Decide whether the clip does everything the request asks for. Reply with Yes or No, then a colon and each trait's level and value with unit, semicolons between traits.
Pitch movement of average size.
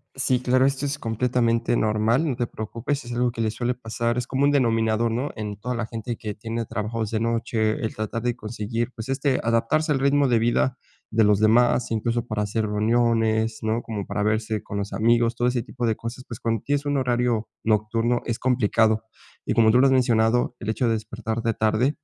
No: narrow, 2.0 semitones